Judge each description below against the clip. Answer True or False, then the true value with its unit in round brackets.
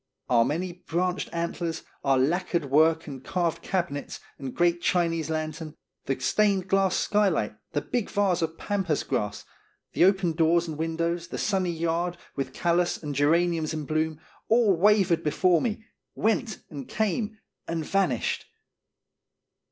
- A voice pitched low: False (170 Hz)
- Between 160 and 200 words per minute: False (145 wpm)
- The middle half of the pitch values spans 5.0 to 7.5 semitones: False (2.9 semitones)